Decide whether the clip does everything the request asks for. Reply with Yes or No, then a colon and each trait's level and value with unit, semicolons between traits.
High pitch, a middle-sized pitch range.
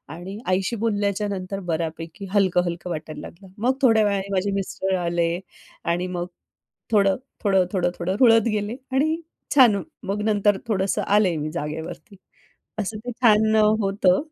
Yes: high, 195 Hz; average, 3.2 semitones